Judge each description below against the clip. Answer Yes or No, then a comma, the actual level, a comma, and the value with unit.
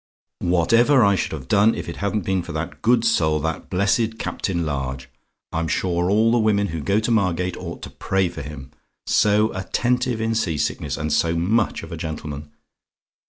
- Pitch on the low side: Yes, very low, 95 Hz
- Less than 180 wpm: No, average, 190 wpm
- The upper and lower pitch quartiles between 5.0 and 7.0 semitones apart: Yes, average, 5.3 semitones